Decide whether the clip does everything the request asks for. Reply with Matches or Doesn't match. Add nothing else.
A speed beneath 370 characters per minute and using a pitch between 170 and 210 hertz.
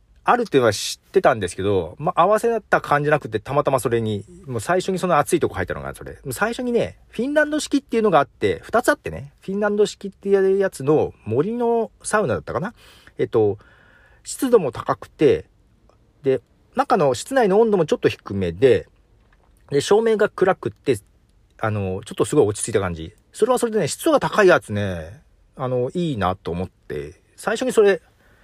Doesn't match